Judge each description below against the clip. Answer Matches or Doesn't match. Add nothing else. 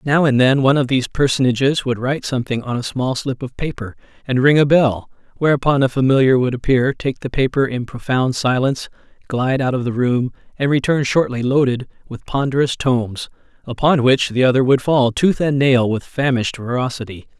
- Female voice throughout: Doesn't match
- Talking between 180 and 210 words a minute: Matches